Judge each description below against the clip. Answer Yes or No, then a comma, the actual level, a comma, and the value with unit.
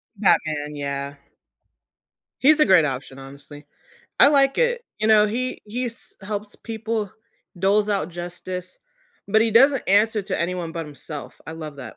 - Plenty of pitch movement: Yes, wide, 6.3 semitones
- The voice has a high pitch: Yes, high, 195 Hz